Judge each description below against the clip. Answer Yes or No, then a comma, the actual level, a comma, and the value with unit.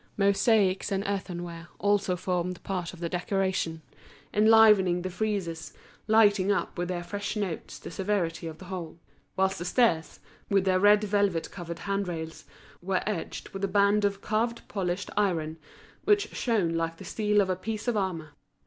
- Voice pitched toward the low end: No, high, 190 Hz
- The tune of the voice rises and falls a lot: No, average, 2.9 semitones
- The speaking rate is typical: Yes, average, 165 wpm